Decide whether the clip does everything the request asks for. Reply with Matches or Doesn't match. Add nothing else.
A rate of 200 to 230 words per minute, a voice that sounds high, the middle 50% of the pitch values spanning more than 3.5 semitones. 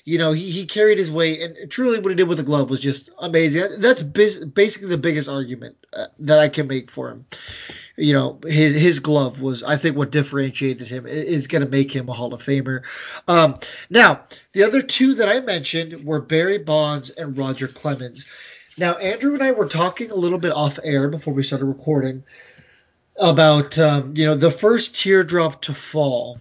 Doesn't match